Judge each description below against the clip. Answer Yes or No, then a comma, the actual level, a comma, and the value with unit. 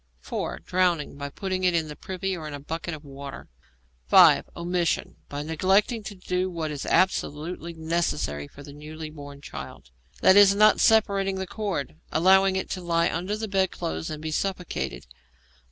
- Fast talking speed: No, average, 170 wpm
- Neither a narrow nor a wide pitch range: Yes, average, 4.3 semitones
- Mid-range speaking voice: Yes, medium, 170 Hz